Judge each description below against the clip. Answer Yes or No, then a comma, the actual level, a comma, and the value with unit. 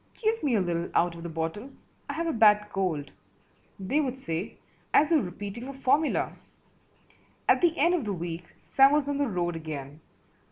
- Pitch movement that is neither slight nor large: No, wide, 8.8 semitones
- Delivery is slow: No, average, 190 wpm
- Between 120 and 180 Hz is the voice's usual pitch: No, high, 210 Hz